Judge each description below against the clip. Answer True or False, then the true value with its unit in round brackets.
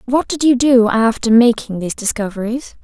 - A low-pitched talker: False (235 Hz)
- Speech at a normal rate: True (170 wpm)